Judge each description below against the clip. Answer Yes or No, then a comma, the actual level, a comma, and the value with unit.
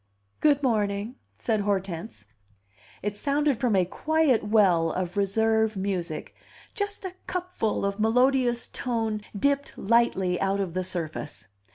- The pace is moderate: No, slow, 130 wpm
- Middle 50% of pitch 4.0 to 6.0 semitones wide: Yes, average, 4.8 semitones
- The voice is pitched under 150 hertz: No, high, 215 Hz